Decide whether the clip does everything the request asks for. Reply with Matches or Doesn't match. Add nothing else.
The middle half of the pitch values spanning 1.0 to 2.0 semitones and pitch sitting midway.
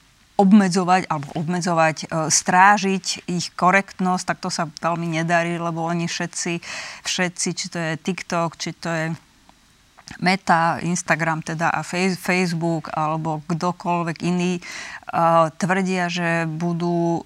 Matches